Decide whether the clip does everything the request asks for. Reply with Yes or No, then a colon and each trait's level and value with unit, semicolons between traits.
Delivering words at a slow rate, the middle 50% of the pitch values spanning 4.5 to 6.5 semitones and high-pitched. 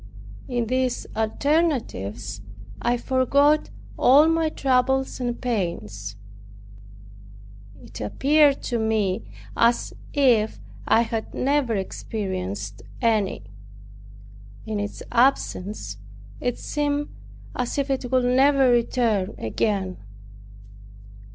Yes: slow, 95 wpm; average, 4.8 semitones; high, 240 Hz